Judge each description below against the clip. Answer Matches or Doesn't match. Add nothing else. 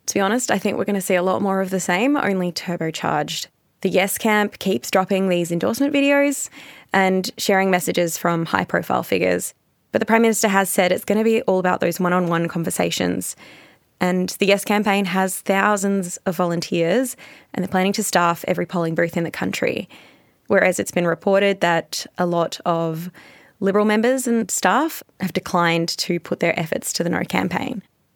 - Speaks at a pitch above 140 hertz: Matches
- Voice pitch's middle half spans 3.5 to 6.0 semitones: Doesn't match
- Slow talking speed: Doesn't match